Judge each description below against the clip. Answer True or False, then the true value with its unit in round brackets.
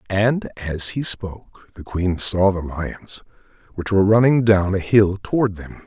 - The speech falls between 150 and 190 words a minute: True (175 wpm)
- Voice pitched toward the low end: True (100 Hz)